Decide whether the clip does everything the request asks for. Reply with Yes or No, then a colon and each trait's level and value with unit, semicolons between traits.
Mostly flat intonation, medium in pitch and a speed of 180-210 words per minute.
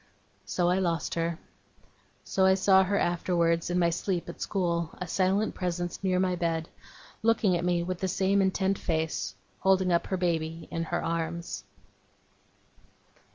No: narrow, 2.0 semitones; medium, 175 Hz; average, 155 wpm